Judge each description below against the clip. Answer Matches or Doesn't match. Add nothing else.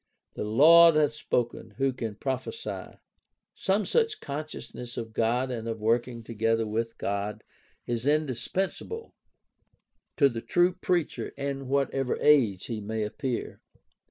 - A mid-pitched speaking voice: Doesn't match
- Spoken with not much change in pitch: Doesn't match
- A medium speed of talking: Doesn't match